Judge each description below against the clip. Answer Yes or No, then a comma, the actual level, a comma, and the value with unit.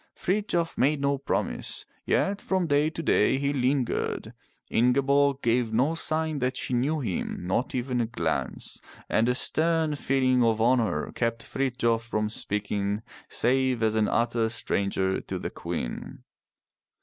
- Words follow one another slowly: No, average, 145 wpm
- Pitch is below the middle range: Yes, low, 125 Hz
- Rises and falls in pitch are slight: No, average, 3.8 semitones